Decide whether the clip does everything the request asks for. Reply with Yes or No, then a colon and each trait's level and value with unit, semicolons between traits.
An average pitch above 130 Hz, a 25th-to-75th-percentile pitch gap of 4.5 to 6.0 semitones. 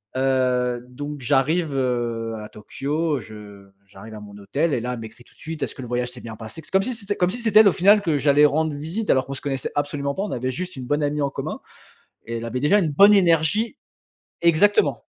Yes: medium, 140 Hz; average, 5.3 semitones